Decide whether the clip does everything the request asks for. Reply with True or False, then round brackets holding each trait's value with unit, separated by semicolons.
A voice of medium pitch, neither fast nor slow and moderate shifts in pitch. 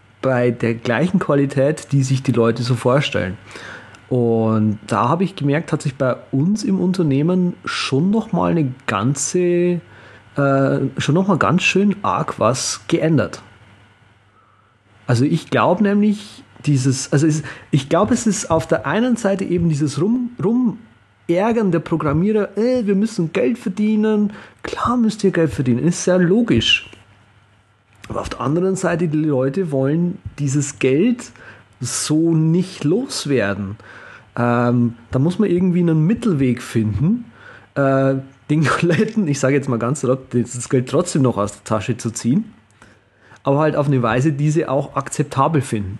False (145 Hz; 155 wpm; 6.7 semitones)